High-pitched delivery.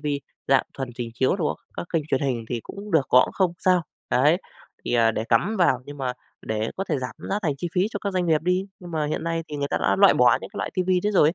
No: medium, 155 Hz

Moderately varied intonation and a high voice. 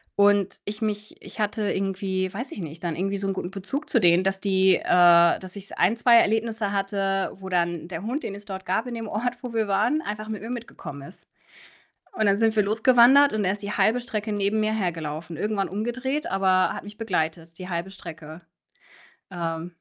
Yes: average, 3.1 semitones; high, 200 Hz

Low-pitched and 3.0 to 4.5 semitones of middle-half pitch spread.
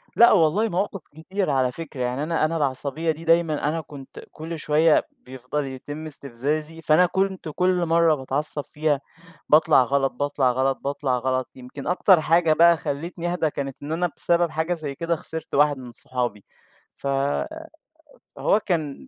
No: medium, 155 Hz; average, 3.4 semitones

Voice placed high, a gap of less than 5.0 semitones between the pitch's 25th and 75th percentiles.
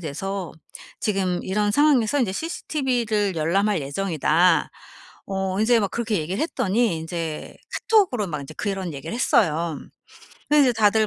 No: high, 195 Hz; average, 5.3 semitones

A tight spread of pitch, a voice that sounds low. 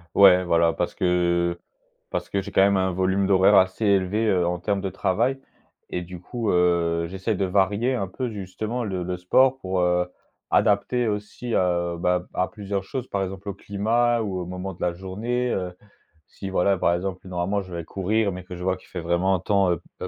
Yes: narrow, 2.3 semitones; very low, 95 Hz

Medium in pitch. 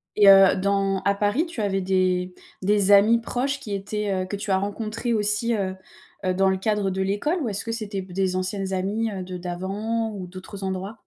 No: high, 200 Hz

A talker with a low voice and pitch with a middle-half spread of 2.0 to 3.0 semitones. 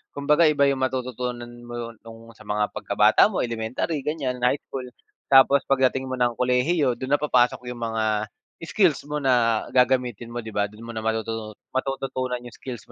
Yes: low, 125 Hz; average, 2.7 semitones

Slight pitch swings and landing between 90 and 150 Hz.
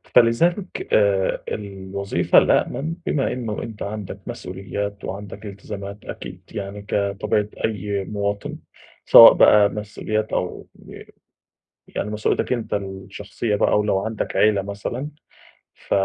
Yes: narrow, 1.5 semitones; low, 105 Hz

